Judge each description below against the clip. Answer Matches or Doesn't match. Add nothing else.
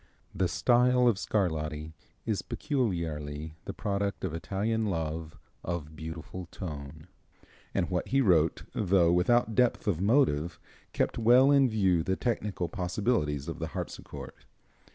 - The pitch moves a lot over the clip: Matches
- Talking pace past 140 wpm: Doesn't match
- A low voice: Matches